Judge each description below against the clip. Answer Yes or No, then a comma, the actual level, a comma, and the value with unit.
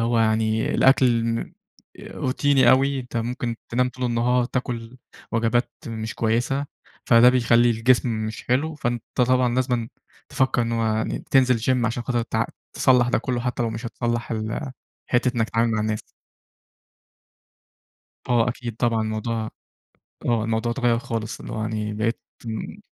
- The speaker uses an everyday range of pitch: No, narrow, 1.7 semitones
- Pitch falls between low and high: No, low, 120 Hz